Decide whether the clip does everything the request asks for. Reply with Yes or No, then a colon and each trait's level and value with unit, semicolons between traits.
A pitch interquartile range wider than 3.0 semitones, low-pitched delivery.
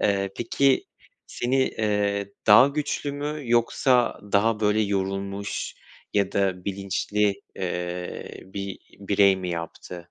No: average, 2.7 semitones; low, 100 Hz